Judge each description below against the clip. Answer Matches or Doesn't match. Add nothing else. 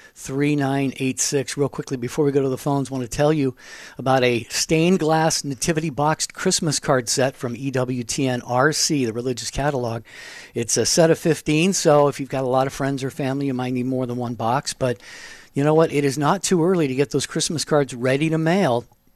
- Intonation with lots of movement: Doesn't match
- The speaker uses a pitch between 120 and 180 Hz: Matches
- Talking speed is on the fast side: Matches